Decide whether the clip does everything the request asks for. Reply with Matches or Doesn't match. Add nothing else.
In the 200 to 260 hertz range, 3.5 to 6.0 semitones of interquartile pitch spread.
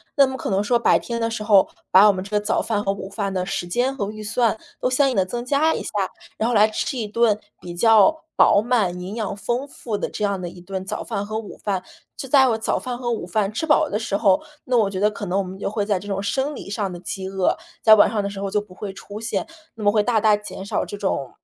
Doesn't match